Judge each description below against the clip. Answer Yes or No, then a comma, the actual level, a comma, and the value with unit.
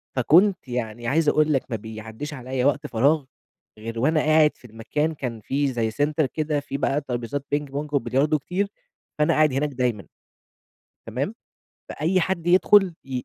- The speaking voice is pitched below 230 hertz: Yes, medium, 140 Hz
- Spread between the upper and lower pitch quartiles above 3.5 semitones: Yes, average, 3.9 semitones